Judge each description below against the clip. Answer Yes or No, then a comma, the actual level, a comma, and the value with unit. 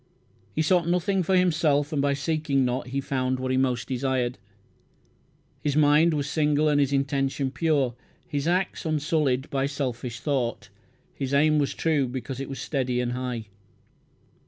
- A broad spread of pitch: No, average, 3.0 semitones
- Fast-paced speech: No, average, 160 wpm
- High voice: No, medium, 140 Hz